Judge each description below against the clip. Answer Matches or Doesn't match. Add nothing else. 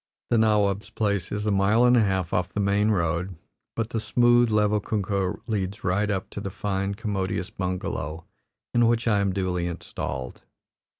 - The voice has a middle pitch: Doesn't match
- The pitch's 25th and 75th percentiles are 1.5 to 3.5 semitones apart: Matches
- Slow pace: Doesn't match